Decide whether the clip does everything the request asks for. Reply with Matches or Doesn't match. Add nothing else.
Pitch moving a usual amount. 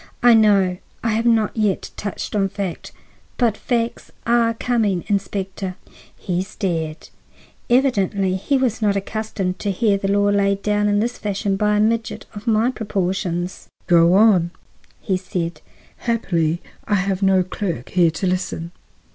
Matches